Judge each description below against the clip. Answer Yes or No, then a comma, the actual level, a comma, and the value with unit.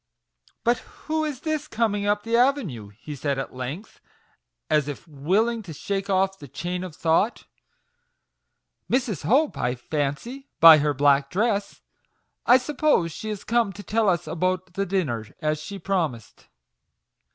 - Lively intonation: Yes, wide, 7.3 semitones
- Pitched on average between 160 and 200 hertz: Yes, medium, 185 Hz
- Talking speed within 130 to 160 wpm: No, average, 170 wpm